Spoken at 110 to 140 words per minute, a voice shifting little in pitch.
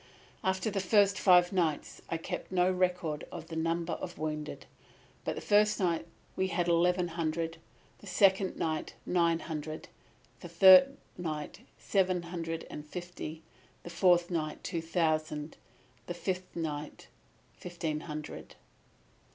Yes: slow, 135 wpm; narrow, 2.3 semitones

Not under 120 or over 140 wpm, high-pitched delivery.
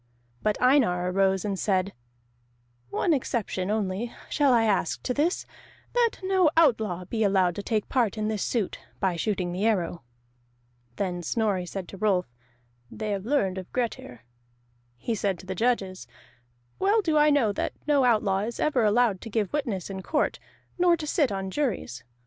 No: average, 170 wpm; high, 210 Hz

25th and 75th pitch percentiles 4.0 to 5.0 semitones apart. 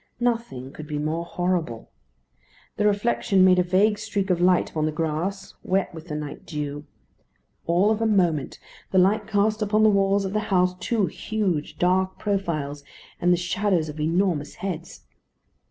Yes: average, 4.3 semitones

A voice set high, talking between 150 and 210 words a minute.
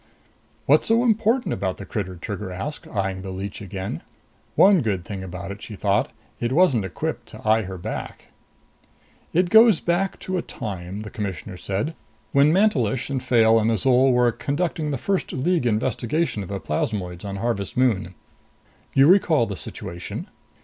No: low, 110 Hz; average, 165 wpm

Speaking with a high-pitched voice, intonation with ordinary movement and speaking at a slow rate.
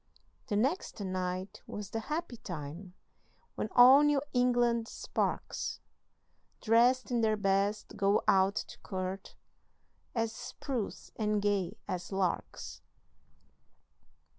Yes: high, 210 Hz; average, 4.0 semitones; slow, 110 wpm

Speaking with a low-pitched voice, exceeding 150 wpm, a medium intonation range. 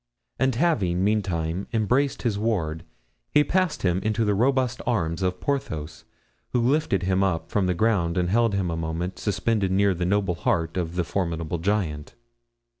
Yes: very low, 95 Hz; average, 170 wpm; average, 4.9 semitones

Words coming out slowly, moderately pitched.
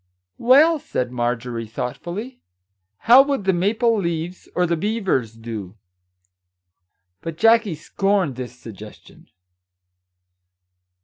Yes: slow, 100 wpm; medium, 170 Hz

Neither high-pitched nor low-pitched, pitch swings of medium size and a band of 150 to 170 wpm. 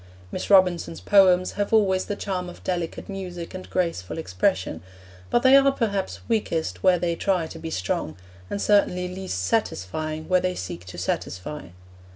Yes: medium, 180 Hz; average, 3.7 semitones; average, 165 wpm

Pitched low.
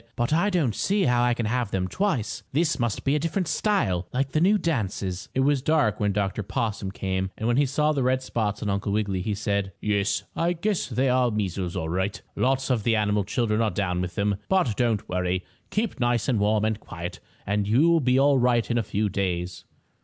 Yes: low, 115 Hz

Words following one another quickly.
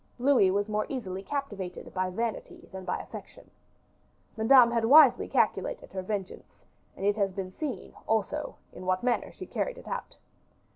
No: average, 155 wpm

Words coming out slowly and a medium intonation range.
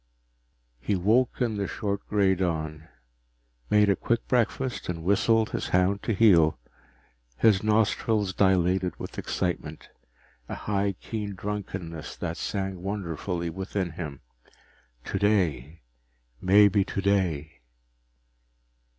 Yes: slow, 105 wpm; average, 3.2 semitones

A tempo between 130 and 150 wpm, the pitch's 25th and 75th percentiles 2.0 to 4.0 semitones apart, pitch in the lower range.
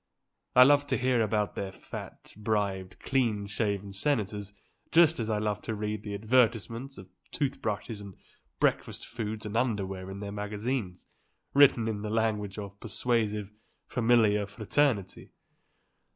Yes: average, 140 wpm; average, 2.7 semitones; low, 105 Hz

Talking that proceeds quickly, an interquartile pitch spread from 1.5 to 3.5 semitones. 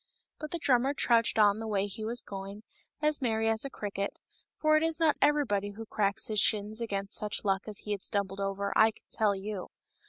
Yes: fast, 215 wpm; average, 3.1 semitones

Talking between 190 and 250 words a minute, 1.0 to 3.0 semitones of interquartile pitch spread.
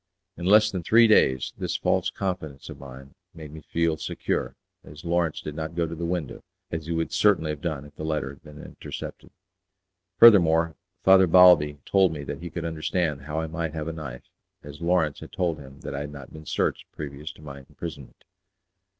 Yes: average, 200 wpm; average, 2.7 semitones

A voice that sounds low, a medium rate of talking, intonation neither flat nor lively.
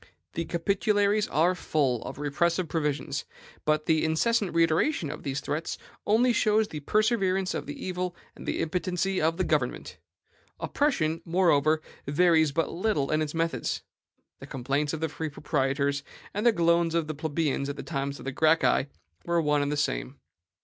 No: medium, 160 Hz; average, 170 wpm; average, 3.7 semitones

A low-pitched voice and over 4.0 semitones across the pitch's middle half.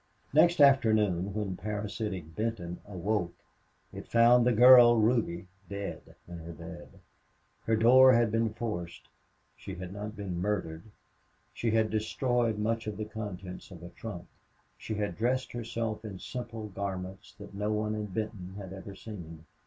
No: low, 105 Hz; average, 3.4 semitones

